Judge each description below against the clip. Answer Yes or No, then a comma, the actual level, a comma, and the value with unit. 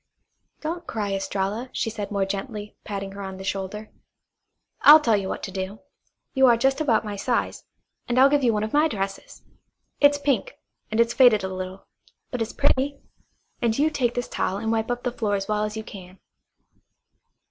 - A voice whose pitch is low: No, high, 220 Hz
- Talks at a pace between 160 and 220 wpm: Yes, average, 195 wpm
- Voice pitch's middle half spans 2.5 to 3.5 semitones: No, average, 4.4 semitones